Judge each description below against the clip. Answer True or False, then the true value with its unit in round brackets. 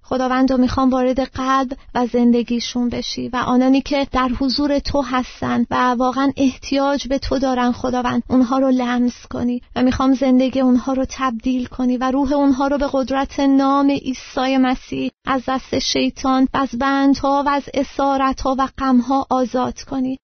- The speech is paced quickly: True (160 wpm)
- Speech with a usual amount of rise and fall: False (1.5 semitones)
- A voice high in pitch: True (260 Hz)